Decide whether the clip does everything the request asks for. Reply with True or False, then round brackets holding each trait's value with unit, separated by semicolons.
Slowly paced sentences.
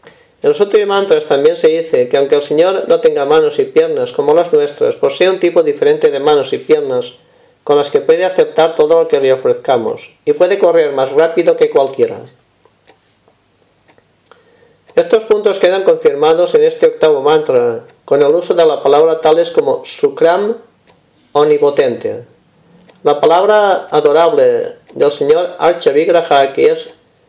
False (155 wpm)